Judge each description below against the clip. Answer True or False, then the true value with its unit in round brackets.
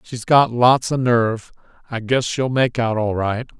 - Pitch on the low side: True (120 Hz)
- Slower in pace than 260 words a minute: True (200 wpm)